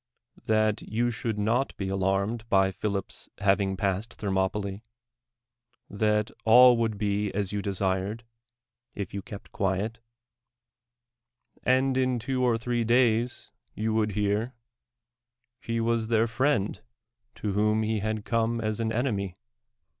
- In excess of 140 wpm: No, slow, 135 wpm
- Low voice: Yes, low, 110 Hz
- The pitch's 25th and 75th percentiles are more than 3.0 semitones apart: No, average, 2.7 semitones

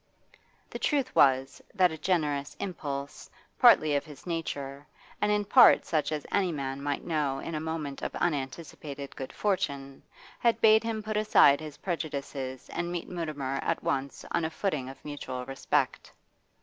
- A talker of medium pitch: Yes, medium, 150 Hz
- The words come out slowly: No, average, 160 wpm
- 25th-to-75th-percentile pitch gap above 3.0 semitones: Yes, average, 4.2 semitones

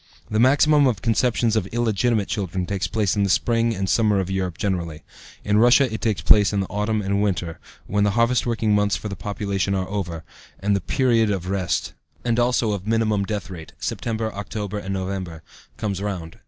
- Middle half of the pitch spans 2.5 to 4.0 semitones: Yes, average, 2.8 semitones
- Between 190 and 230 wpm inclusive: Yes, average, 195 wpm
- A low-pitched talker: Yes, low, 105 Hz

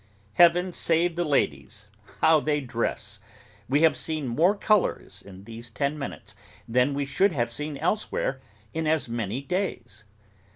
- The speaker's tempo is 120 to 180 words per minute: Yes, average, 150 wpm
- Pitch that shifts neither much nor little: No, wide, 6.0 semitones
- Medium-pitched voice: Yes, medium, 145 Hz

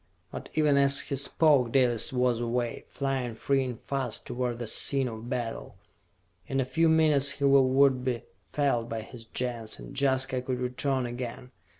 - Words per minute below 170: No, average, 175 wpm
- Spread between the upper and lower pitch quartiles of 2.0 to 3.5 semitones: Yes, narrow, 2.4 semitones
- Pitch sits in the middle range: No, low, 130 Hz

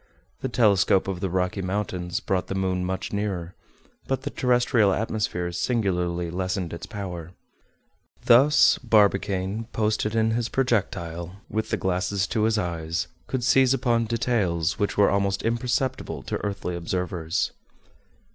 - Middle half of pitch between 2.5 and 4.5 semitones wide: Yes, average, 3.8 semitones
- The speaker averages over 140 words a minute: No, slow, 135 wpm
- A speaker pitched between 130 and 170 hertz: No, low, 100 Hz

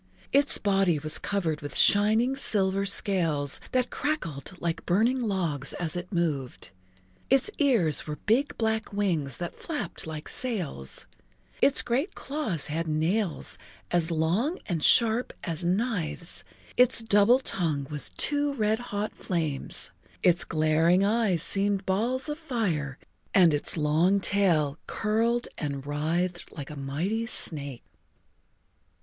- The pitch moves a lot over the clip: Yes, wide, 6.3 semitones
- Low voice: No, medium, 185 Hz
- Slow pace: Yes, slow, 130 wpm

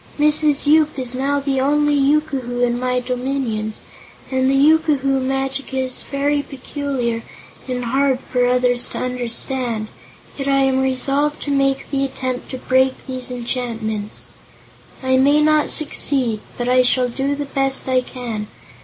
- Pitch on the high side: Yes, very high, 265 Hz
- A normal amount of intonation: No, narrow, 1.9 semitones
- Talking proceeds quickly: No, average, 150 wpm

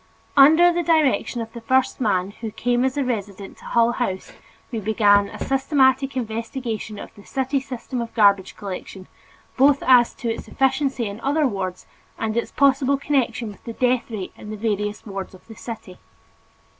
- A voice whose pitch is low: No, high, 235 Hz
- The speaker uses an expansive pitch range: No, average, 4.3 semitones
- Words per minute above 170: Yes, average, 180 wpm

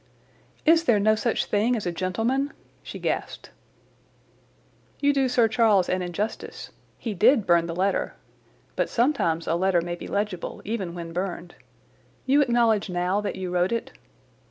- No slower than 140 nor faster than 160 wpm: Yes, average, 155 wpm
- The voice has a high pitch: Yes, high, 205 Hz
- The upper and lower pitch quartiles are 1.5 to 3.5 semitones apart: No, average, 4.9 semitones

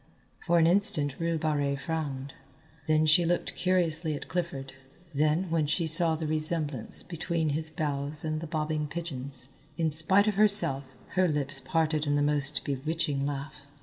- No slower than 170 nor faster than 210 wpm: No, average, 160 wpm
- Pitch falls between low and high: Yes, medium, 155 Hz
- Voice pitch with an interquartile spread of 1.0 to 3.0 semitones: Yes, narrow, 2.5 semitones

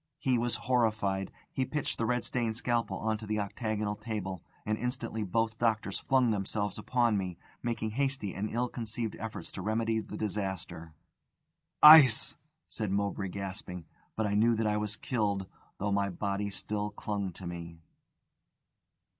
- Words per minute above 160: No, average, 155 wpm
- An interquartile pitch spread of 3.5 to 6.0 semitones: No, narrow, 2.6 semitones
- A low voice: Yes, low, 105 Hz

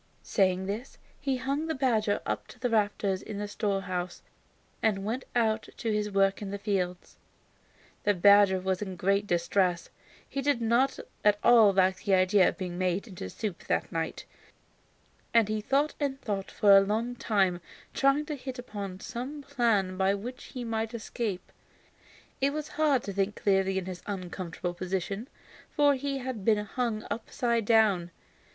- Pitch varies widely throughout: No, average, 4.1 semitones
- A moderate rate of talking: Yes, average, 170 wpm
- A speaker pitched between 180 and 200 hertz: No, high, 210 Hz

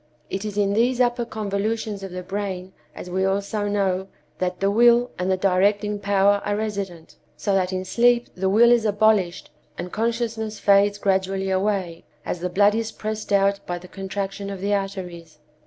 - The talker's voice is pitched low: No, high, 200 Hz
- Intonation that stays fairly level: Yes, narrow, 2.0 semitones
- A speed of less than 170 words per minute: No, average, 180 wpm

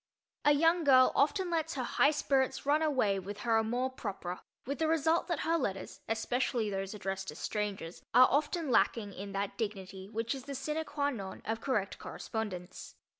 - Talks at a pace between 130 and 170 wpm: No, average, 180 wpm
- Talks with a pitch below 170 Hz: No, high, 240 Hz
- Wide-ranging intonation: Yes, wide, 6.2 semitones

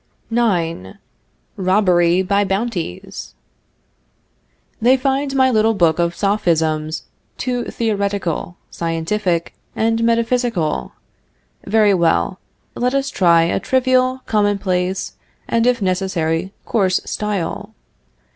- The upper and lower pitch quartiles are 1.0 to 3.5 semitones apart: No, average, 5.1 semitones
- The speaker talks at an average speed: No, slow, 95 wpm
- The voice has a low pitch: No, high, 200 Hz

